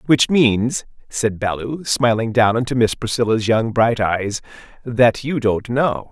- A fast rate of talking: No, average, 155 wpm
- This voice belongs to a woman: No, male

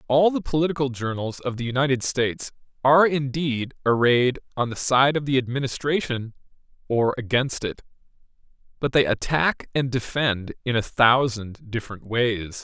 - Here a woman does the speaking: No, male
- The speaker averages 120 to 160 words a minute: Yes, average, 140 wpm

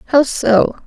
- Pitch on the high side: Yes, very high, 260 Hz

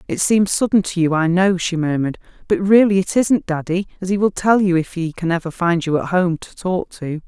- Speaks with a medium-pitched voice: Yes, medium, 180 Hz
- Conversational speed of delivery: No, fast, 240 wpm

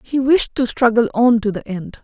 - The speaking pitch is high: Yes, high, 230 Hz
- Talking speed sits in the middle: No, fast, 235 wpm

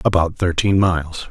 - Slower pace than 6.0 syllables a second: Yes, 5.0 syllables/s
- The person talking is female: No, male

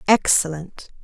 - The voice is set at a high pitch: No, medium, 175 Hz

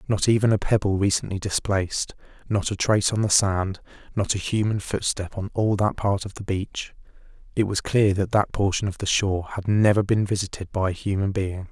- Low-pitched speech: Yes, low, 100 Hz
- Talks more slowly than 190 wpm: No, fast, 205 wpm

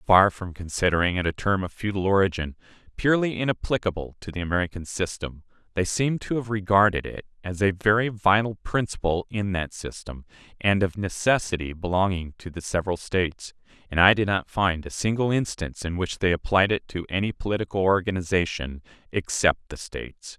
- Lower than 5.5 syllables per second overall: No, 5.6 syllables/s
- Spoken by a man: Yes, male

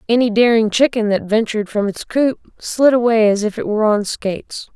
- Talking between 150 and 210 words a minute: Yes, average, 200 wpm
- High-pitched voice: Yes, high, 220 Hz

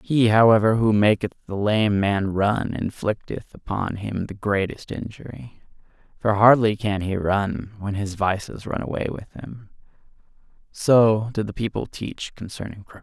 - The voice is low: Yes, low, 105 Hz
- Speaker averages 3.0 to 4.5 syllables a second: Yes, 4.4 syllables/s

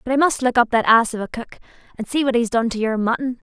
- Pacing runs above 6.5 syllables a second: Yes, 6.8 syllables/s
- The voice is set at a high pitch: Yes, high, 240 Hz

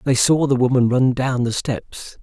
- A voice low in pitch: Yes, low, 130 Hz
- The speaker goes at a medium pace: No, fast, 215 wpm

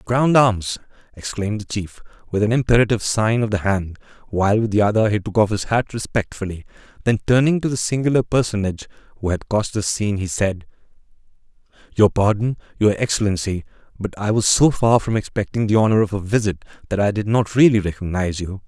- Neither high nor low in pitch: No, low, 105 Hz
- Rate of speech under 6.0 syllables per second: No, 6.1 syllables/s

